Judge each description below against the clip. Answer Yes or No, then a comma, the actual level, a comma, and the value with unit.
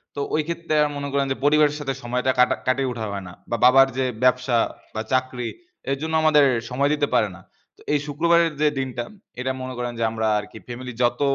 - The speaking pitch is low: Yes, low, 130 Hz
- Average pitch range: Yes, average, 3.0 semitones